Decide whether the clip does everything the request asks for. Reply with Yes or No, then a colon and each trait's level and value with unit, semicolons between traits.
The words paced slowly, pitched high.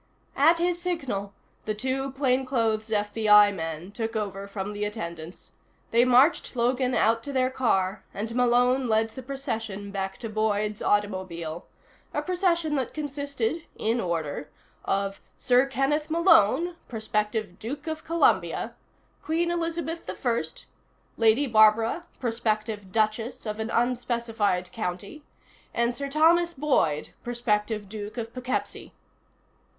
Yes: slow, 125 wpm; high, 230 Hz